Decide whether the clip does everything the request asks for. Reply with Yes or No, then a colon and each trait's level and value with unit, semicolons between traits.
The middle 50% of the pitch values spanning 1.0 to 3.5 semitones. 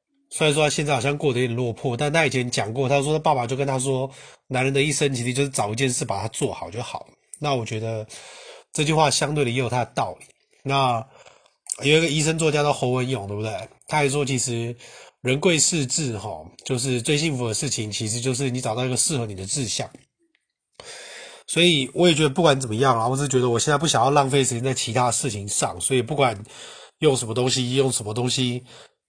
Yes: average, 3.2 semitones